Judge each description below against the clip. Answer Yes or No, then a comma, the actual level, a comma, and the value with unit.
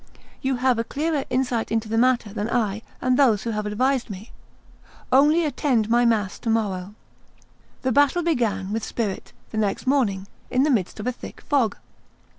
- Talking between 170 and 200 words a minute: Yes, average, 180 wpm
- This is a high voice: Yes, high, 235 Hz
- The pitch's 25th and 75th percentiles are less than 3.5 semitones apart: No, average, 3.8 semitones